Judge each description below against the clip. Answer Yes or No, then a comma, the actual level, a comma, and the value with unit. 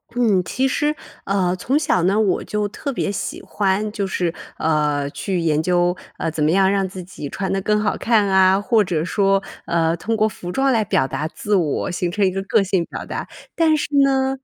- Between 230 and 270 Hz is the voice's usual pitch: No, high, 195 Hz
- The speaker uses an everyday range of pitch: Yes, average, 3.4 semitones